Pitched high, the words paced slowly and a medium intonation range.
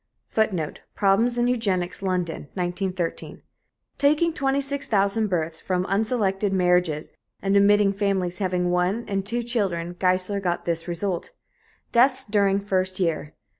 Yes: high, 195 Hz; slow, 125 wpm; average, 3.3 semitones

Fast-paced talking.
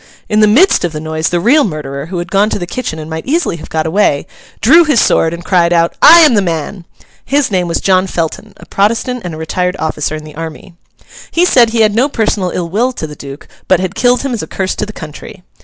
Yes: fast, 255 wpm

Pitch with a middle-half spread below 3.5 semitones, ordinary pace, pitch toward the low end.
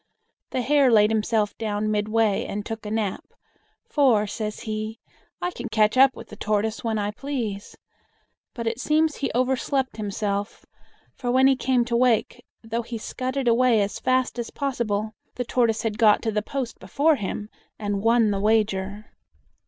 No: average, 3.1 semitones; average, 170 wpm; high, 225 Hz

